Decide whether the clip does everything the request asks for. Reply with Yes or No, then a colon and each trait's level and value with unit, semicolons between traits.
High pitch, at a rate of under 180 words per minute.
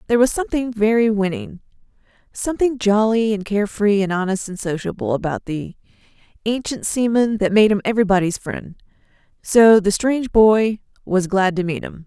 Yes: high, 210 Hz; average, 150 wpm